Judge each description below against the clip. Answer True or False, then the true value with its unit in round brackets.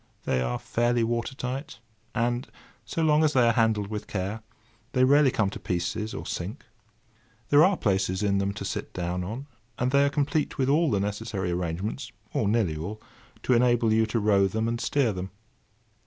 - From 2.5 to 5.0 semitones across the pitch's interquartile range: True (4.5 semitones)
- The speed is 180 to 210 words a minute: True (185 wpm)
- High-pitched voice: False (110 Hz)